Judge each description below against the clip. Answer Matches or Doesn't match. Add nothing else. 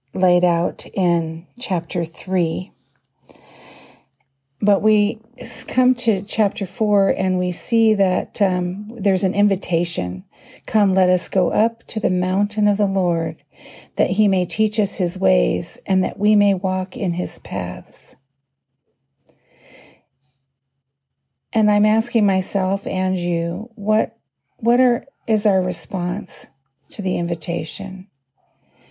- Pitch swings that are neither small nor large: Matches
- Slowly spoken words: Matches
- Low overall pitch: Doesn't match